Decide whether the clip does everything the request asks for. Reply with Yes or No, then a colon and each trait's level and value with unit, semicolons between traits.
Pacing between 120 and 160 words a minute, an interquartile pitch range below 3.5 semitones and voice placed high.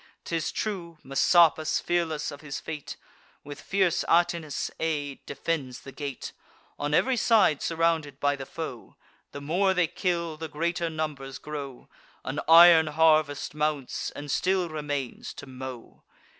No: average, 140 wpm; average, 2.9 semitones; medium, 155 Hz